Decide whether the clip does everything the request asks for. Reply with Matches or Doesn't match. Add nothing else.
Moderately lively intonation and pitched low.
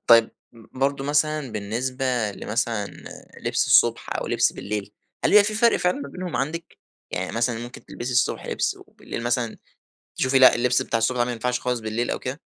Matches